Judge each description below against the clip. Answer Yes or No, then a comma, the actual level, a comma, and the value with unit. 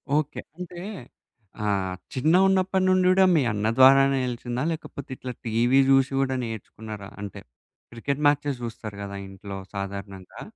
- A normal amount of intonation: No, wide, 6.0 semitones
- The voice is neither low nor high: No, low, 125 Hz